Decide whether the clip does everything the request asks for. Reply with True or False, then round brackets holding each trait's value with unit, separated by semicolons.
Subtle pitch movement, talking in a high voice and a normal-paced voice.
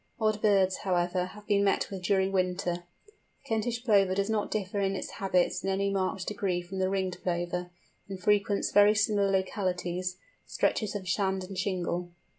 True (1.9 semitones; 195 Hz; 175 wpm)